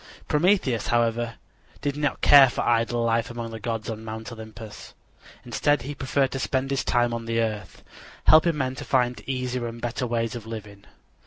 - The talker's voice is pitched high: No, low, 120 Hz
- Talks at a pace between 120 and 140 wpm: No, average, 180 wpm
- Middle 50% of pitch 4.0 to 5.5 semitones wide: No, narrow, 2.6 semitones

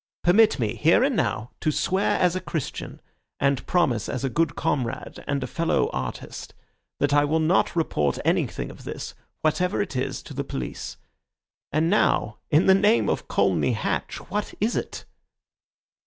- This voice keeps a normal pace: Yes, average, 170 wpm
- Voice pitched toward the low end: No, medium, 155 Hz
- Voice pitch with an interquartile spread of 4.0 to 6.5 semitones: Yes, wide, 5.5 semitones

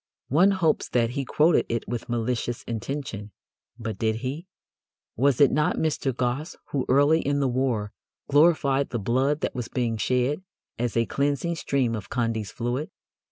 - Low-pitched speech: Yes, low, 130 Hz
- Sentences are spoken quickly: No, average, 160 wpm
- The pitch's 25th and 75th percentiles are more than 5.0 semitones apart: No, average, 3.7 semitones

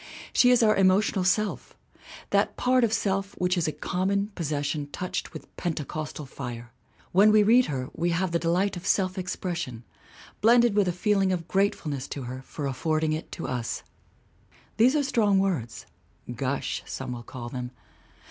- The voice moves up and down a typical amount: No, wide, 5.9 semitones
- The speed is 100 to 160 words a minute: No, average, 175 wpm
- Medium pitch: Yes, medium, 180 Hz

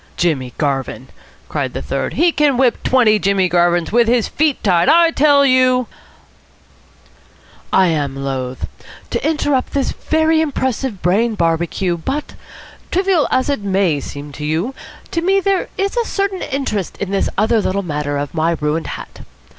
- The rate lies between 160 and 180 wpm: Yes, average, 170 wpm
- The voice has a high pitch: Yes, high, 215 Hz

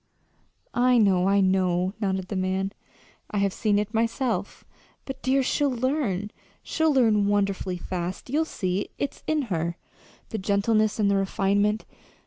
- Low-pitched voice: No, high, 205 Hz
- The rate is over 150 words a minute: No, average, 145 wpm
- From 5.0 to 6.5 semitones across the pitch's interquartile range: No, average, 3.9 semitones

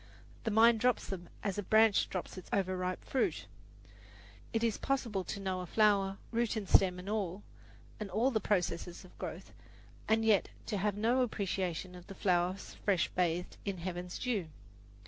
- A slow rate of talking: No, average, 170 wpm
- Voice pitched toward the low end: No, high, 195 Hz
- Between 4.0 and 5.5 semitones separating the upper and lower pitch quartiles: No, average, 3.2 semitones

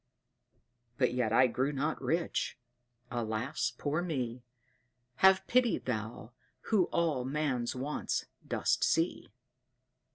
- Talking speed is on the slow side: Yes, slow, 105 wpm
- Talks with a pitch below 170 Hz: Yes, low, 135 Hz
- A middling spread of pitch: Yes, average, 5.0 semitones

